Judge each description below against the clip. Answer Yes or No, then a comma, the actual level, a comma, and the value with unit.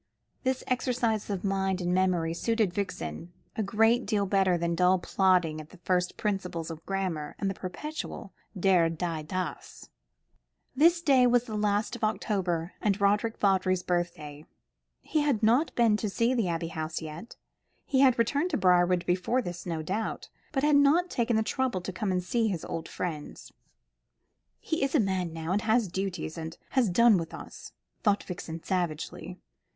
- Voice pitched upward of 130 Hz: Yes, high, 190 Hz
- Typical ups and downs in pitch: Yes, average, 4.7 semitones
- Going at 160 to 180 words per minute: Yes, average, 170 wpm